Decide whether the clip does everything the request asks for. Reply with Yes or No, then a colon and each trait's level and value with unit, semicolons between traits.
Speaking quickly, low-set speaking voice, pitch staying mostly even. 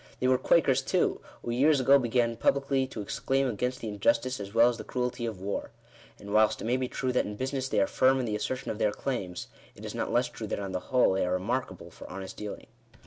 No: fast, 255 wpm; low, 120 Hz; average, 3.9 semitones